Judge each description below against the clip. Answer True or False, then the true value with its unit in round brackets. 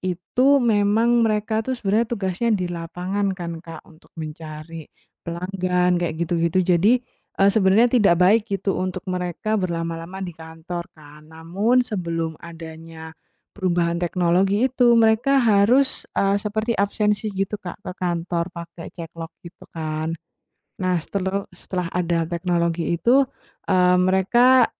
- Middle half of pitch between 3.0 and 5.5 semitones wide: True (3.7 semitones)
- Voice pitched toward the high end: False (180 Hz)